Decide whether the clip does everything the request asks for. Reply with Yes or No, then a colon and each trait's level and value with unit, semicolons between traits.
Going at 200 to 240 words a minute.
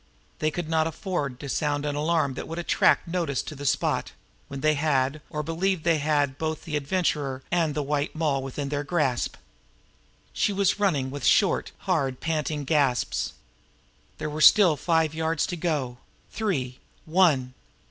No: average, 170 wpm